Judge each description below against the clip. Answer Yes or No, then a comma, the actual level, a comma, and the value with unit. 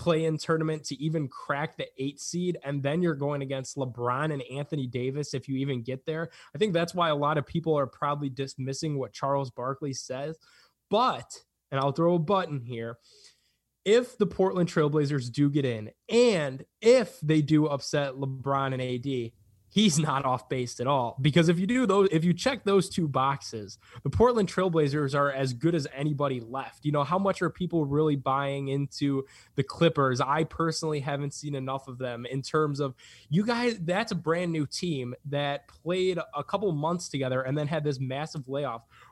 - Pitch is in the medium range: Yes, medium, 145 Hz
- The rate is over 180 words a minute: Yes, average, 195 wpm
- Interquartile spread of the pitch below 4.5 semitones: Yes, average, 3.7 semitones